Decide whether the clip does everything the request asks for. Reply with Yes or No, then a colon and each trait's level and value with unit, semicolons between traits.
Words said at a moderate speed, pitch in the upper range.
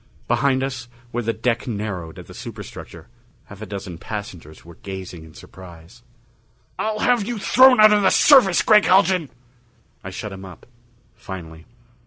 No: average, 160 wpm; low, 110 Hz